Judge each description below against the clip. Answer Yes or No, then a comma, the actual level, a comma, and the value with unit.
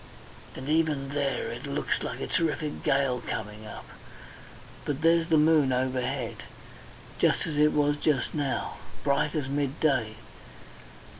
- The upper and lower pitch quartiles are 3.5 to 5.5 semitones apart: No, average, 2.7 semitones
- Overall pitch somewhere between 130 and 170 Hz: Yes, medium, 140 Hz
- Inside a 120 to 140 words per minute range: Yes, slow, 135 wpm